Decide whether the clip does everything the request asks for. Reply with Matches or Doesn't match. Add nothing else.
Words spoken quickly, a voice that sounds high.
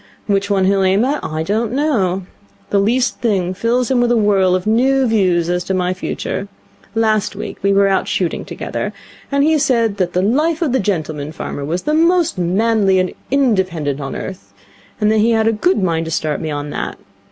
Matches